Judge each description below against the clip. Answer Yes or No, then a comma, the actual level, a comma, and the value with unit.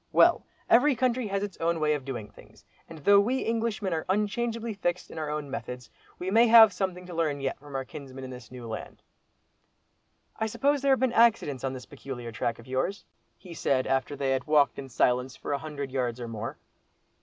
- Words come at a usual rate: No, fast, 215 wpm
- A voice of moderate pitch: Yes, medium, 150 Hz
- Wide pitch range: Yes, wide, 7.9 semitones